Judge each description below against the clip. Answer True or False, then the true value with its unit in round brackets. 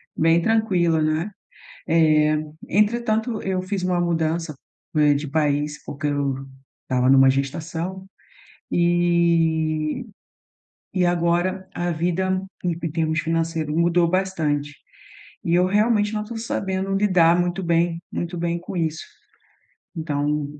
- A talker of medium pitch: True (170 Hz)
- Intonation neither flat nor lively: True (3.1 semitones)